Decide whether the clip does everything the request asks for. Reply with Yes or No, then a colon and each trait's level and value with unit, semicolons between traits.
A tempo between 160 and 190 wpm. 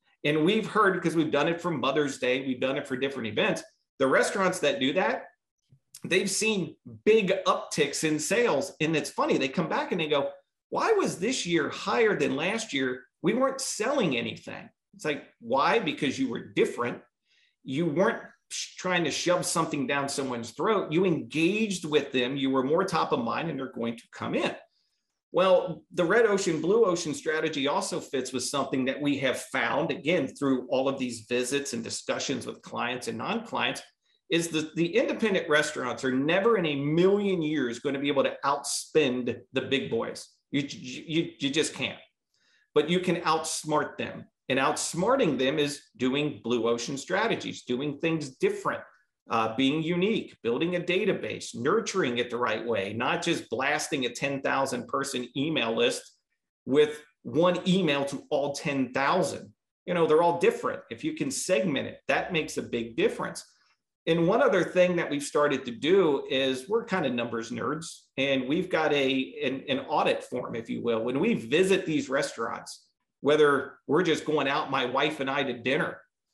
Yes: average, 180 wpm